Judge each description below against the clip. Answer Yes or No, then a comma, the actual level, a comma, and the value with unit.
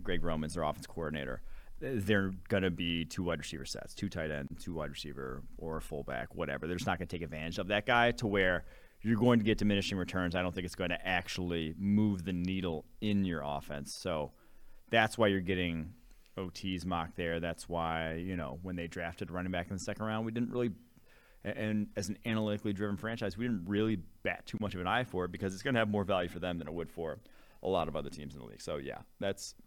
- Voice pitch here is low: Yes, very low, 90 Hz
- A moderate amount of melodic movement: Yes, average, 3.9 semitones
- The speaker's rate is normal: No, fast, 240 wpm